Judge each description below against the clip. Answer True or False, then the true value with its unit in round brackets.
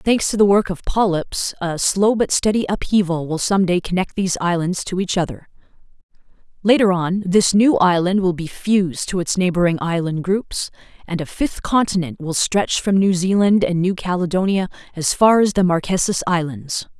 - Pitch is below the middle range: False (185 Hz)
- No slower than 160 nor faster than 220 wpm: True (175 wpm)